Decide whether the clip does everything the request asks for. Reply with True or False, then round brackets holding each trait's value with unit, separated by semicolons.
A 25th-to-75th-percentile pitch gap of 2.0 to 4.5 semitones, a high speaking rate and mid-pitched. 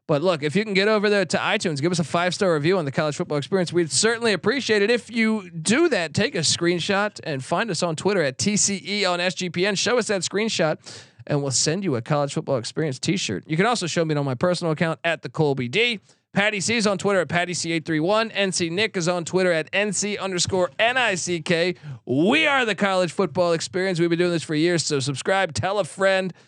True (3.7 semitones; 240 wpm; 180 Hz)